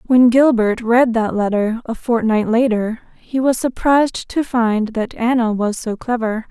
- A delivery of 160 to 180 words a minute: Yes, average, 165 wpm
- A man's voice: No, female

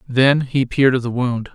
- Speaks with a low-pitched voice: Yes, low, 130 Hz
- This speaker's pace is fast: Yes, fast, 235 wpm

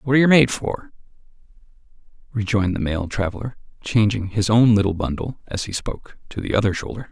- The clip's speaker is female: No, male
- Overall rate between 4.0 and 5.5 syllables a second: No, 6.1 syllables/s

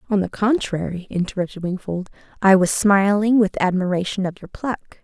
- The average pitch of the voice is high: Yes, high, 195 Hz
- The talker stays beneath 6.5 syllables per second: Yes, 5.4 syllables/s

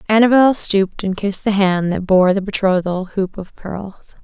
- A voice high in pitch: Yes, high, 195 Hz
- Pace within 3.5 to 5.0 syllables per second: Yes, 4.8 syllables/s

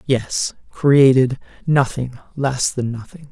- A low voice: Yes, low, 130 Hz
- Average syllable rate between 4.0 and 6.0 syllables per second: No, 3.5 syllables/s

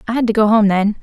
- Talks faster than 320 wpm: Yes, fast, 350 wpm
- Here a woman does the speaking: Yes, female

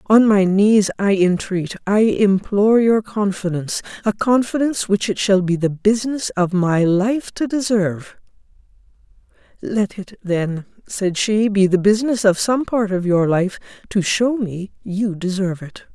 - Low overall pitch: No, high, 200 Hz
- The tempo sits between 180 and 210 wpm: No, average, 160 wpm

